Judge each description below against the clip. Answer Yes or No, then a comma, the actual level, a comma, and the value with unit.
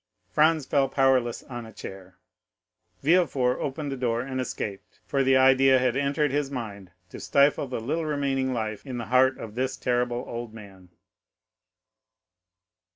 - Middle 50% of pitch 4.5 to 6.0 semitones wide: No, average, 2.8 semitones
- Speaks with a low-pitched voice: Yes, low, 130 Hz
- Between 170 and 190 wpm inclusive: No, average, 155 wpm